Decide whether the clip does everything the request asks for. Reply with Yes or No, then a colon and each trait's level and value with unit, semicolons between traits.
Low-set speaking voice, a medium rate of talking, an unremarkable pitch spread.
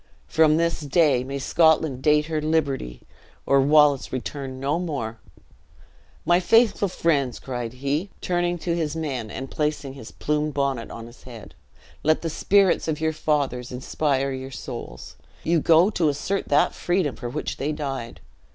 No: medium, 150 Hz; average, 160 wpm; average, 3.4 semitones